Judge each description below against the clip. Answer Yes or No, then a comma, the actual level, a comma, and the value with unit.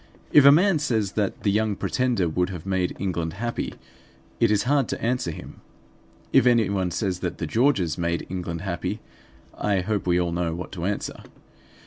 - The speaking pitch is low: Yes, very low, 95 Hz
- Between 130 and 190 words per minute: Yes, average, 180 wpm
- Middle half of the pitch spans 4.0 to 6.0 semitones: Yes, average, 4.8 semitones